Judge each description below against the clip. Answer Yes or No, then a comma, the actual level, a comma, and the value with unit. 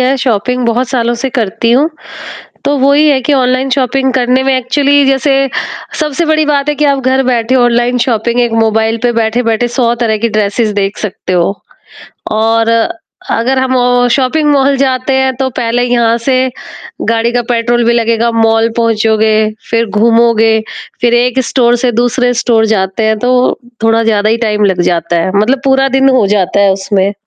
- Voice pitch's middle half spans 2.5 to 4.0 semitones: Yes, average, 2.8 semitones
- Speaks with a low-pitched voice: No, high, 240 Hz